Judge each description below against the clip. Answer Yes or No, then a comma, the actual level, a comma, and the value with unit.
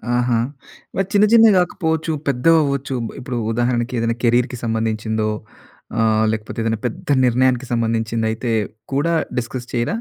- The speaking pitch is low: Yes, low, 120 Hz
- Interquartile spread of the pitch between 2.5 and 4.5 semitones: Yes, average, 3.5 semitones